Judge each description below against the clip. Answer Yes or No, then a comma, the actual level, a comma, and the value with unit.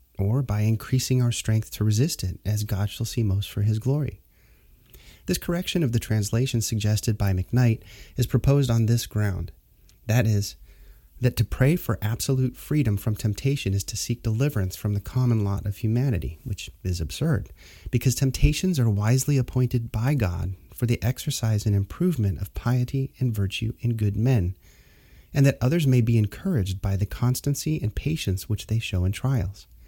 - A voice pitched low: Yes, low, 110 Hz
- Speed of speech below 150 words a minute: No, average, 175 wpm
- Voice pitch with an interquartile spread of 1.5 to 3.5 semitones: No, average, 4.3 semitones